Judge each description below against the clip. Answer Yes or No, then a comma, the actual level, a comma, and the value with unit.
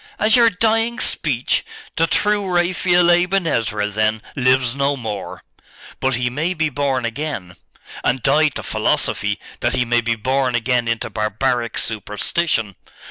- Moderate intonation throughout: No, wide, 6.8 semitones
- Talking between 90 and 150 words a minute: Yes, average, 145 wpm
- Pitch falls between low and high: No, low, 130 Hz